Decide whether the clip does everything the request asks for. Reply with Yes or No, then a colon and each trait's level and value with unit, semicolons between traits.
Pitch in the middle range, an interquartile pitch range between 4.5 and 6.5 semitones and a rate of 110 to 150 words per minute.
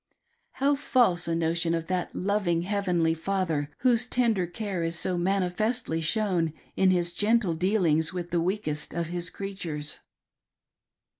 No: medium, 180 Hz; average, 3.3 semitones; average, 140 wpm